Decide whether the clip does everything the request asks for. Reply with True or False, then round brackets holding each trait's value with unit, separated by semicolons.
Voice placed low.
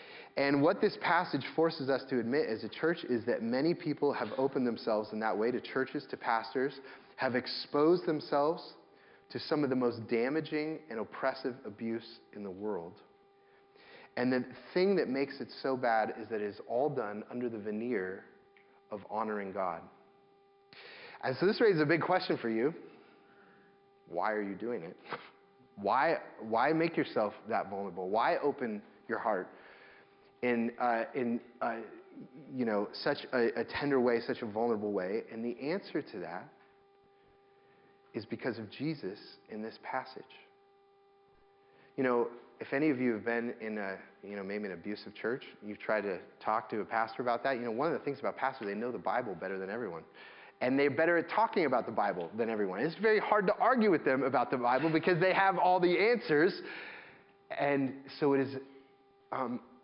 True (130 Hz)